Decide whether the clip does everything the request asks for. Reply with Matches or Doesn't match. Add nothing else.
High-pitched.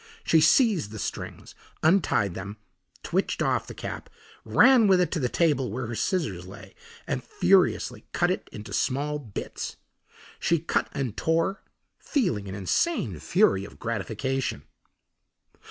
Doesn't match